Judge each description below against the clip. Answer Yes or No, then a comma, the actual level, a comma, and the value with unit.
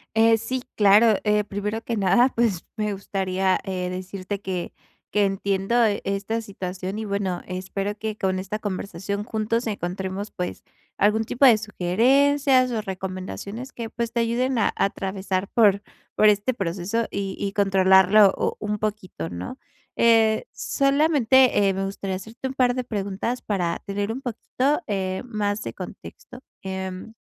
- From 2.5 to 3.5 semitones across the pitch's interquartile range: Yes, average, 3.1 semitones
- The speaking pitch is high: Yes, high, 205 Hz